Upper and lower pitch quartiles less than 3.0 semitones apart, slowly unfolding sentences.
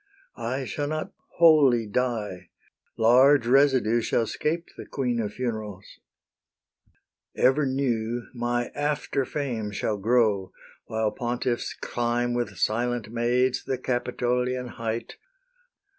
Yes: narrow, 2.5 semitones; slow, 110 wpm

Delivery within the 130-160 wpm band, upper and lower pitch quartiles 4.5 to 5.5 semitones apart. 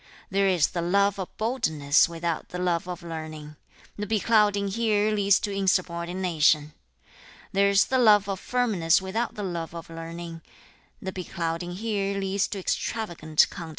No: average, 150 wpm; average, 3.4 semitones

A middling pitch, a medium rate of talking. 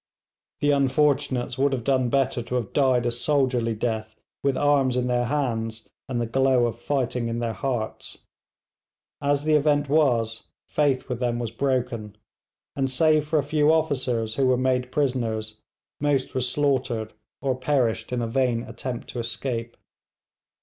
No: low, 130 Hz; average, 160 wpm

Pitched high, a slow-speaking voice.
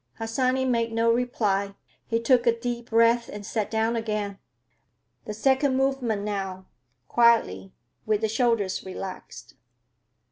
Yes: high, 230 Hz; slow, 130 wpm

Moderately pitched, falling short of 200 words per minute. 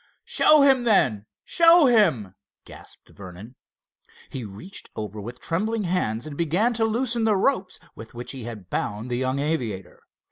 Yes: medium, 150 Hz; average, 155 wpm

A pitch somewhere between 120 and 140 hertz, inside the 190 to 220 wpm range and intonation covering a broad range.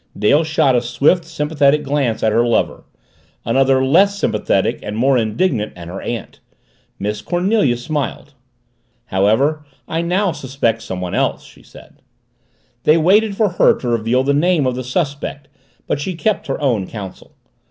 No: low, 135 Hz; average, 155 wpm; wide, 5.8 semitones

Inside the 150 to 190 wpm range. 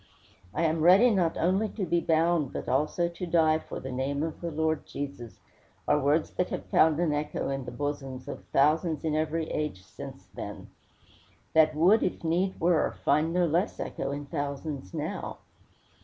Yes: average, 180 wpm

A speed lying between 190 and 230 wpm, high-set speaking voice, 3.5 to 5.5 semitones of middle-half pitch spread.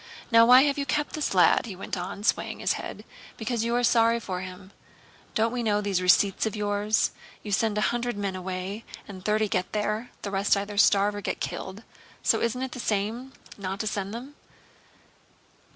No: average, 200 wpm; high, 210 Hz; average, 2.9 semitones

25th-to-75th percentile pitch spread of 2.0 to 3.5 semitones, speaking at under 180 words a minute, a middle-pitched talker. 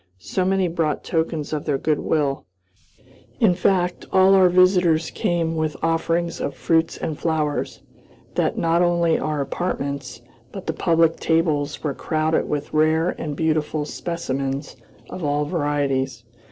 Yes: average, 2.7 semitones; average, 140 wpm; medium, 160 Hz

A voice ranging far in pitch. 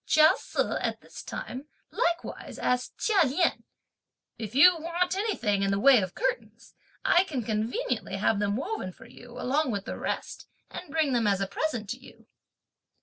Yes: wide, 8.0 semitones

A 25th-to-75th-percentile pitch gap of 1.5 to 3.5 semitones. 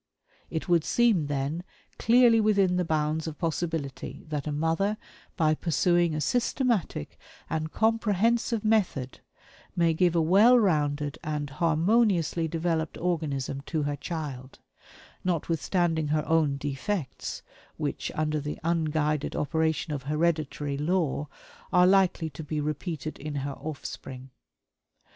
Yes: average, 3.2 semitones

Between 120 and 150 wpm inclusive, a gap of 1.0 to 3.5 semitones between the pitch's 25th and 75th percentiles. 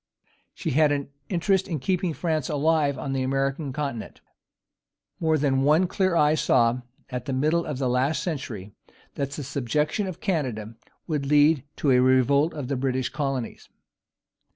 No: average, 160 wpm; average, 3.2 semitones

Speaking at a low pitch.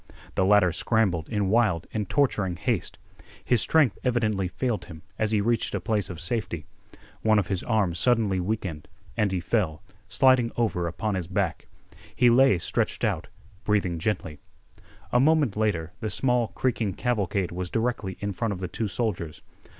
Yes: low, 105 Hz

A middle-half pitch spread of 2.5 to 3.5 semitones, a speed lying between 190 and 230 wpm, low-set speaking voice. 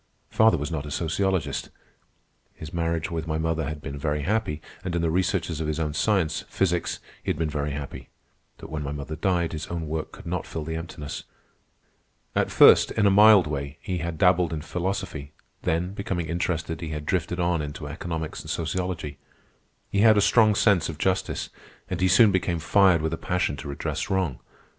Yes: average, 3.2 semitones; average, 195 wpm; very low, 85 Hz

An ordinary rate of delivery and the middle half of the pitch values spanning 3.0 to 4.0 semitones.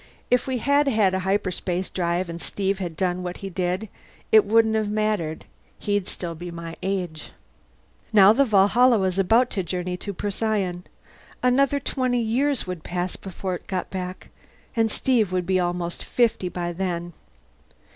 Yes: average, 165 wpm; average, 3.7 semitones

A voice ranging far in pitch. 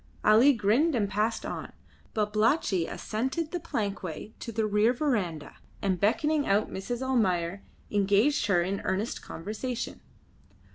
No: average, 4.1 semitones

